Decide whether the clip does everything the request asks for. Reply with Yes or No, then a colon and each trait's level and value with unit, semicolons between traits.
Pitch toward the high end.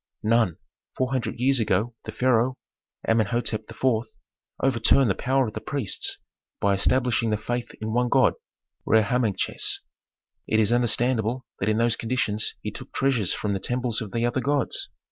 No: low, 115 Hz